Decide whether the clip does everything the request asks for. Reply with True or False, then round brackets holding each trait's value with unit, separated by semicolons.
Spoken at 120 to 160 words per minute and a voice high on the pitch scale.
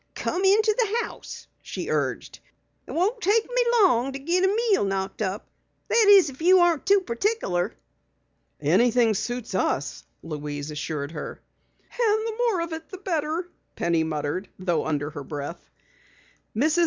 True (155 wpm; 290 Hz)